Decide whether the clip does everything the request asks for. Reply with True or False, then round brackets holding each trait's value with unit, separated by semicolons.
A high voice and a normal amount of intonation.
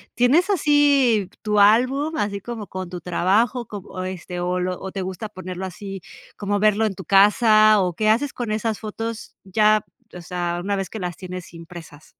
True (205 Hz; 3.4 semitones)